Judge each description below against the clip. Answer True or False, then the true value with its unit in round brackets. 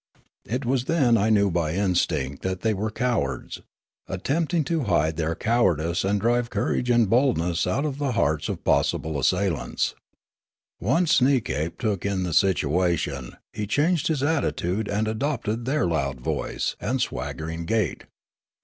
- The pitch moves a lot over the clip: True (6.9 semitones)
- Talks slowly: False (150 wpm)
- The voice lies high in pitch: False (105 Hz)